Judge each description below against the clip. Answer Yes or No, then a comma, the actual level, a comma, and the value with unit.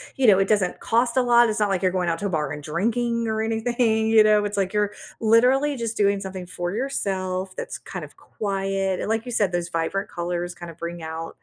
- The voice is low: No, high, 200 Hz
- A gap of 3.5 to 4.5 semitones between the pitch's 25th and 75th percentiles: Yes, average, 4.0 semitones